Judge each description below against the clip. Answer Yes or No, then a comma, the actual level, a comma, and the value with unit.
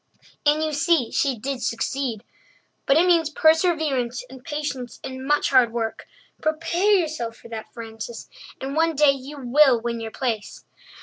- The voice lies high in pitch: Yes, very high, 275 Hz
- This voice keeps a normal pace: Yes, average, 160 wpm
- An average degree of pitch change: Yes, average, 4.6 semitones